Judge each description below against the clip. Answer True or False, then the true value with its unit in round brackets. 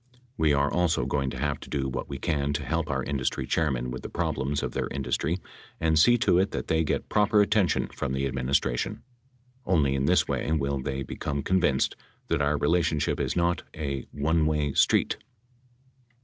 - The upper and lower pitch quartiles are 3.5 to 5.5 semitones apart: False (3.1 semitones)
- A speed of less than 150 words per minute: False (190 wpm)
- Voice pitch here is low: True (75 Hz)